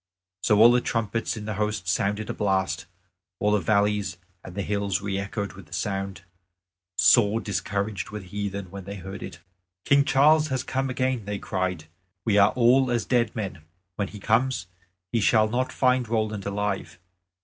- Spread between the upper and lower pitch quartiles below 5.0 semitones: Yes, average, 3.0 semitones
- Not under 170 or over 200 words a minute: Yes, average, 175 wpm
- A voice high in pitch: No, low, 105 Hz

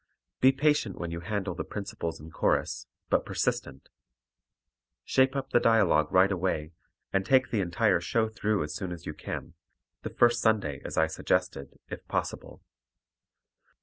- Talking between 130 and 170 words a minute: Yes, average, 155 wpm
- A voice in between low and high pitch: No, very low, 95 Hz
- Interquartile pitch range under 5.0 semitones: No, average, 5.3 semitones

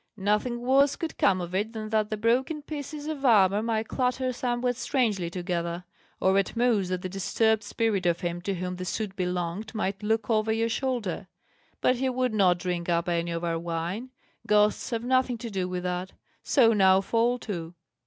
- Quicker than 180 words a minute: Yes, average, 195 wpm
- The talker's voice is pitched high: Yes, high, 210 Hz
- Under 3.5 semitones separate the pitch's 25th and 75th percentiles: No, average, 4.8 semitones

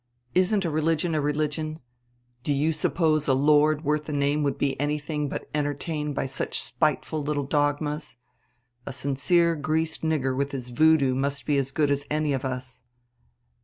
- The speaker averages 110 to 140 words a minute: No, average, 165 wpm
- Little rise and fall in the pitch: Yes, narrow, 1.7 semitones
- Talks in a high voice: No, medium, 150 Hz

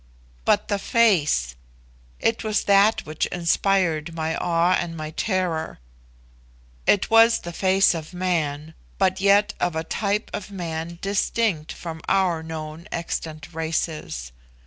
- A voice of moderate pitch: Yes, medium, 170 Hz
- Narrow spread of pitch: No, average, 3.6 semitones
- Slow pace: Yes, slow, 130 wpm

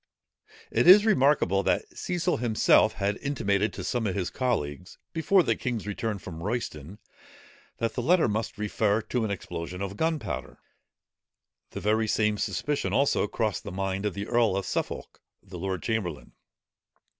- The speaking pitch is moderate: No, low, 105 Hz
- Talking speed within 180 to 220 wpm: No, average, 155 wpm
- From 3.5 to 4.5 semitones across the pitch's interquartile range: Yes, average, 4.0 semitones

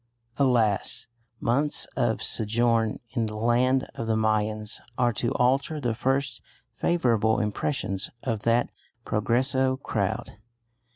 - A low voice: Yes, low, 115 Hz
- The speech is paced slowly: Yes, slow, 115 wpm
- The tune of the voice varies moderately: Yes, average, 3.2 semitones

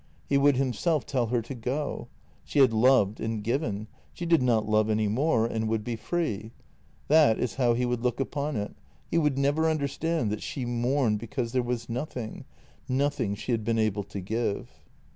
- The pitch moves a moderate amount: Yes, average, 4.0 semitones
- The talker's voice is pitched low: Yes, low, 120 Hz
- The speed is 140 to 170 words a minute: No, average, 195 wpm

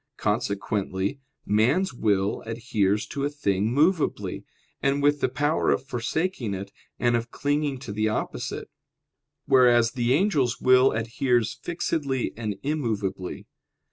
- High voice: No, low, 120 Hz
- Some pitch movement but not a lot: Yes, average, 4.9 semitones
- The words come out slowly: Yes, slow, 125 wpm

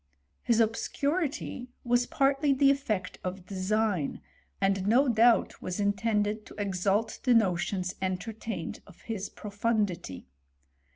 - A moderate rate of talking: No, slow, 115 wpm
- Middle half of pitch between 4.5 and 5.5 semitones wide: No, average, 3.9 semitones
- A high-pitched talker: Yes, high, 215 Hz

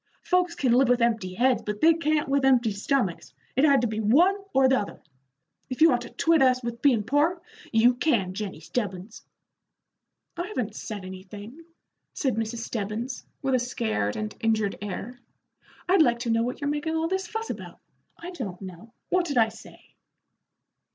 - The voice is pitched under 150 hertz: No, high, 245 Hz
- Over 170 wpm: Yes, average, 185 wpm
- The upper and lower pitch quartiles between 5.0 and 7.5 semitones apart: Yes, wide, 5.4 semitones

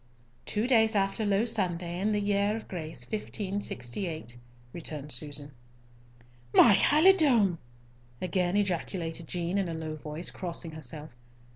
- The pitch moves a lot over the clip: No, average, 4.6 semitones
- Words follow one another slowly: Yes, slow, 125 wpm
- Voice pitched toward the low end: No, medium, 180 Hz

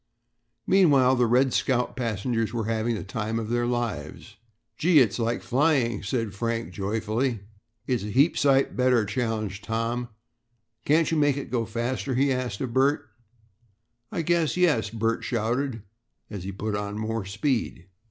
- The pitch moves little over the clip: No, average, 3.3 semitones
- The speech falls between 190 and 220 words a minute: No, average, 155 wpm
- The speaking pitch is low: Yes, low, 120 Hz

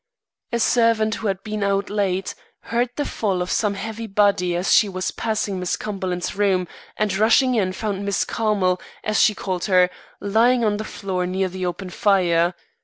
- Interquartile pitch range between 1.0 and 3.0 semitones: Yes, average, 2.7 semitones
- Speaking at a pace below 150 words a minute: No, average, 180 wpm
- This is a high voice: Yes, high, 200 Hz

